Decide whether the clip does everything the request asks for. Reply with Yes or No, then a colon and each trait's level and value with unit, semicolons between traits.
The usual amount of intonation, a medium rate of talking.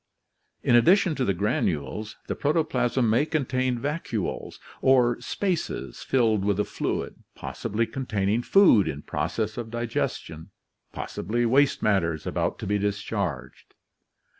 No: average, 4.6 semitones; slow, 130 wpm